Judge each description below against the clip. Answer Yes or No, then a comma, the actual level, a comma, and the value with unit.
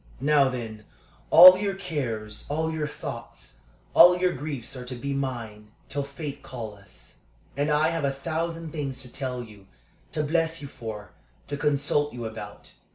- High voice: No, medium, 140 Hz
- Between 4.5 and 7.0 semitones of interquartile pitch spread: Yes, average, 5.0 semitones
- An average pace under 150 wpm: No, average, 165 wpm